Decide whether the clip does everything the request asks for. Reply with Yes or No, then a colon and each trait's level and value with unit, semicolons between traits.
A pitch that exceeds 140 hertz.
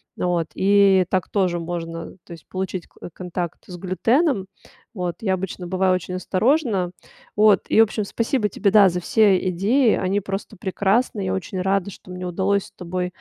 Yes: high, 190 Hz